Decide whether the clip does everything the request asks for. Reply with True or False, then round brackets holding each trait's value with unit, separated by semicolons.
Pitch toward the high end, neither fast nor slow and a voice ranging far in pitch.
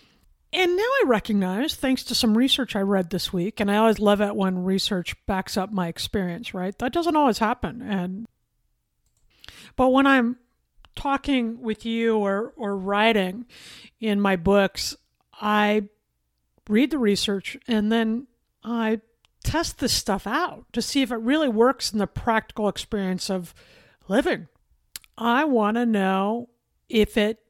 False (220 Hz; 155 wpm; 3.5 semitones)